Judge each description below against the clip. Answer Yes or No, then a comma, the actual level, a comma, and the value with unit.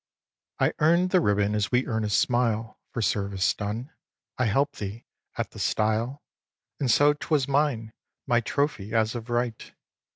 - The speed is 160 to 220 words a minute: Yes, average, 165 wpm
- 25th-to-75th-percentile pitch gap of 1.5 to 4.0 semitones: No, average, 4.4 semitones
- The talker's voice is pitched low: Yes, low, 115 Hz